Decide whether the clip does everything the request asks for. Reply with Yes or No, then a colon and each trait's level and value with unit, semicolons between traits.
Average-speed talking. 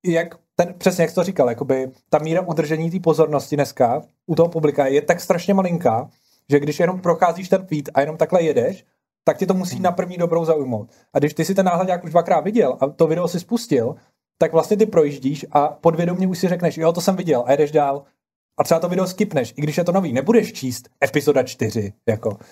No: fast, 225 wpm